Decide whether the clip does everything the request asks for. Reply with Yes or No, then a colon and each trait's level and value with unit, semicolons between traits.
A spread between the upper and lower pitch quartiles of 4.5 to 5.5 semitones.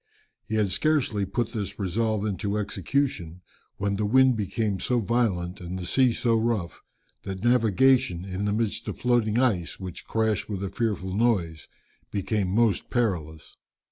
No: average, 3.8 semitones